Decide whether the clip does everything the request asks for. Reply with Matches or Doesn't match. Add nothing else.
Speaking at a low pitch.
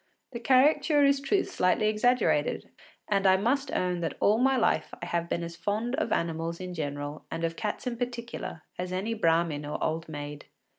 Doesn't match